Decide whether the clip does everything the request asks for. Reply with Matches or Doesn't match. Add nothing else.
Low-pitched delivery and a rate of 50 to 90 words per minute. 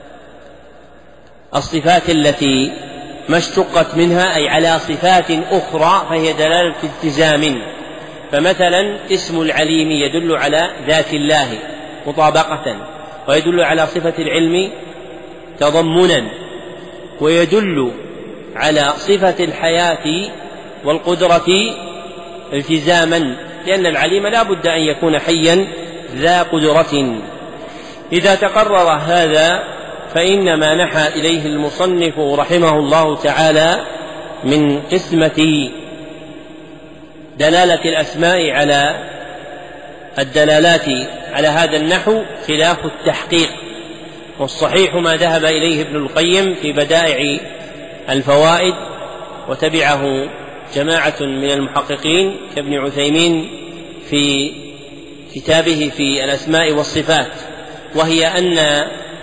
Doesn't match